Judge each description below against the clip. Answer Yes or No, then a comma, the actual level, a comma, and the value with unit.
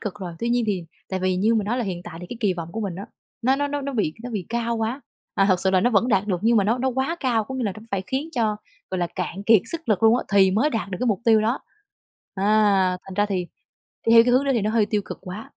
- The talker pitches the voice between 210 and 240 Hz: Yes, high, 215 Hz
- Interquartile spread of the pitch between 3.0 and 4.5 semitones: Yes, average, 3.9 semitones